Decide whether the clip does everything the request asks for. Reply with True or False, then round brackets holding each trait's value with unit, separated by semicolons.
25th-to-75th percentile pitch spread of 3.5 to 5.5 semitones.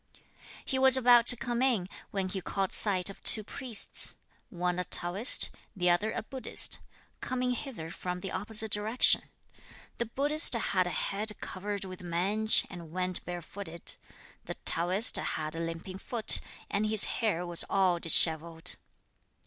True (4.1 semitones)